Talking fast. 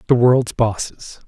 No: average, 140 wpm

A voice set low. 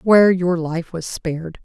No: medium, 170 Hz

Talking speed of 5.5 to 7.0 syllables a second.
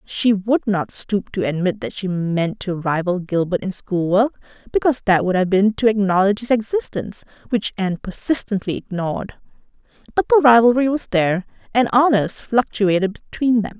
No: 5.3 syllables/s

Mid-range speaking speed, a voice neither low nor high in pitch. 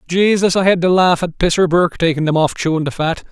No: fast, 255 wpm; medium, 175 Hz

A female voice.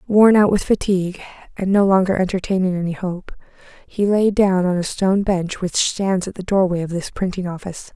Yes: female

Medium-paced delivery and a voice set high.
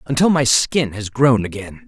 No: average, 190 wpm; low, 130 Hz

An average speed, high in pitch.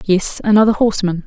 Yes: average, 145 wpm; high, 200 Hz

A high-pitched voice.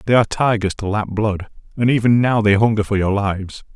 No: low, 105 Hz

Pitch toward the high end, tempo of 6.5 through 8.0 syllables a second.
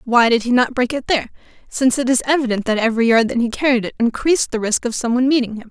Yes: high, 245 Hz; 7.3 syllables/s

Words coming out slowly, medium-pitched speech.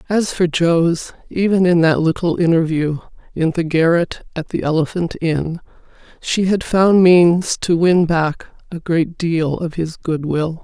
No: average, 165 wpm; medium, 170 Hz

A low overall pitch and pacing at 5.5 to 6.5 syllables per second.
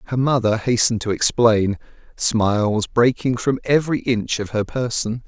No: low, 115 Hz; 4.8 syllables/s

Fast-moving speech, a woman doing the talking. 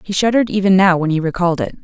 Yes: fast, 260 wpm; female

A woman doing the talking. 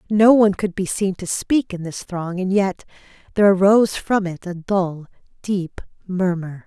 Yes: female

